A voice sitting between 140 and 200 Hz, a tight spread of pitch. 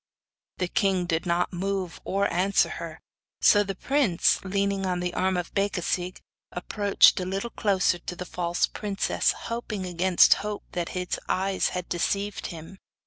Yes: high, 190 Hz; narrow, 1.9 semitones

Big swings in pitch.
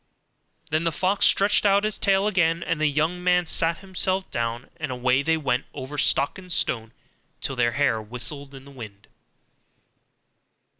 Yes: wide, 6.0 semitones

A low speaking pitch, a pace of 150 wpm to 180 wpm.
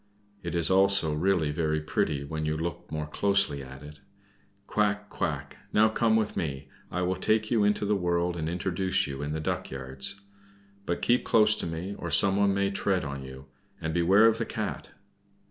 No: very low, 85 Hz; average, 190 wpm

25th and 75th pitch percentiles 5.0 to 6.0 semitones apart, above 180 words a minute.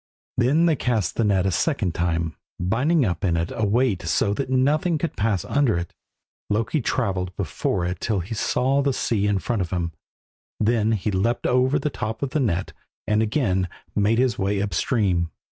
Yes: wide, 5.5 semitones; average, 195 wpm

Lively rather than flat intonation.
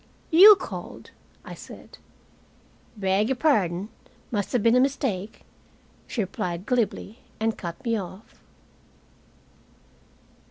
No: average, 4.8 semitones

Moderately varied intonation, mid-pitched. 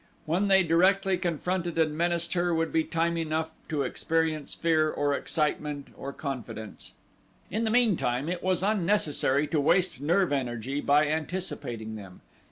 Yes: average, 3.6 semitones; medium, 160 Hz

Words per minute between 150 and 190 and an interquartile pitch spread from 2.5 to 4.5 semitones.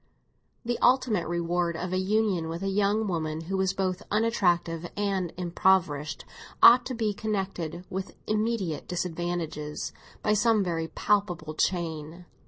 No: slow, 135 wpm; average, 3.7 semitones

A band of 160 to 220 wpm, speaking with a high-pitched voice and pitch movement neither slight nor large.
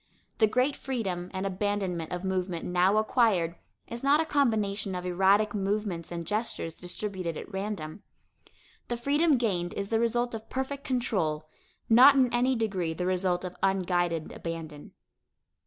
No: average, 150 wpm; high, 195 Hz; average, 4.8 semitones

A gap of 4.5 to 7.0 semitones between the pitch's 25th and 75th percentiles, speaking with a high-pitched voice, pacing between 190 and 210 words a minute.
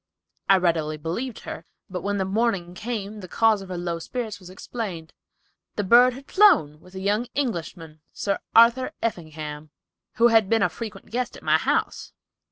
No: average, 5.1 semitones; high, 200 Hz; average, 175 wpm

